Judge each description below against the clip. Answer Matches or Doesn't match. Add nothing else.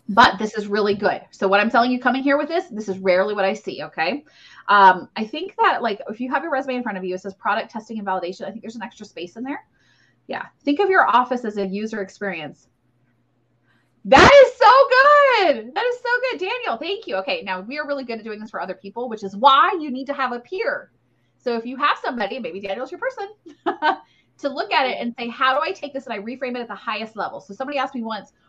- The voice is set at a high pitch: Matches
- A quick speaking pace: Matches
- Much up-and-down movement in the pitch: Matches